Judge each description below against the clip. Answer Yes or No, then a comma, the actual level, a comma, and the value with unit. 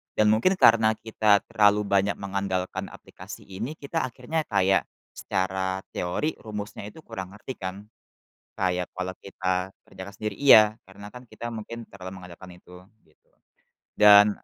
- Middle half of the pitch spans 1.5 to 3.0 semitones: Yes, average, 2.7 semitones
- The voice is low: Yes, low, 100 Hz